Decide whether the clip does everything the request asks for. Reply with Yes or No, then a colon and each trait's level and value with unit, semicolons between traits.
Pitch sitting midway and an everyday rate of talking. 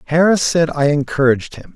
Yes: medium, 150 Hz; average, 170 wpm